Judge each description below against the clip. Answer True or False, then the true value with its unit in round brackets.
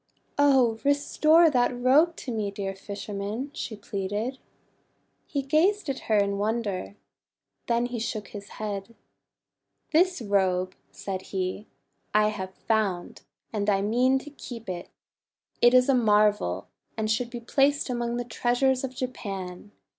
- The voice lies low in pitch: False (225 Hz)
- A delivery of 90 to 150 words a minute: True (140 wpm)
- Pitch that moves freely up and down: False (4.3 semitones)